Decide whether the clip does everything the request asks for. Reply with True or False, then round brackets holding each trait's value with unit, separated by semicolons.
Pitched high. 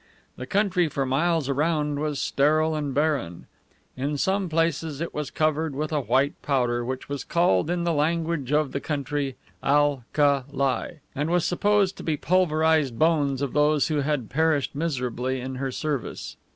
False (150 Hz)